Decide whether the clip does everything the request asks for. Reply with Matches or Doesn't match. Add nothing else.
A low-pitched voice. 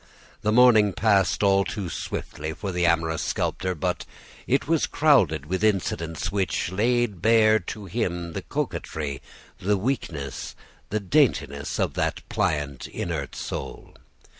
Matches